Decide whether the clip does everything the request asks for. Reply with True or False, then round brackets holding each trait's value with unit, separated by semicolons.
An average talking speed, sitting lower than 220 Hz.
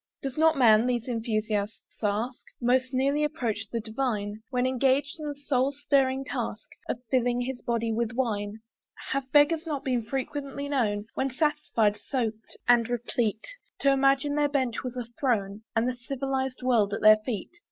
False (165 wpm; 250 Hz)